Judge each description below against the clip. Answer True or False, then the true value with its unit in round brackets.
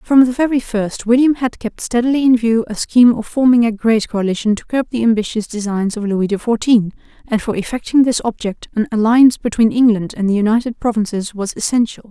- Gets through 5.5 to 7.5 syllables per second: True (5.8 syllables/s)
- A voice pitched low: False (230 Hz)